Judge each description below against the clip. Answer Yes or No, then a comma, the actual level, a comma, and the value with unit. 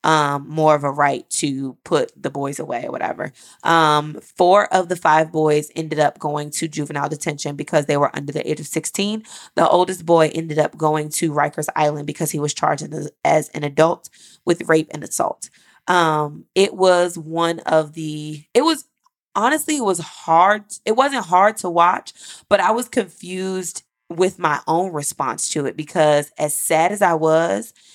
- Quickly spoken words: No, average, 185 wpm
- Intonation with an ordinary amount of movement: Yes, average, 3.2 semitones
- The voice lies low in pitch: No, medium, 160 Hz